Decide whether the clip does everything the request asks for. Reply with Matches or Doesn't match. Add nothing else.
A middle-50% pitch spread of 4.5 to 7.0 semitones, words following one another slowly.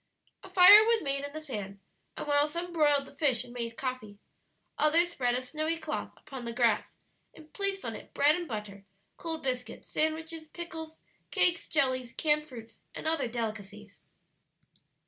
Doesn't match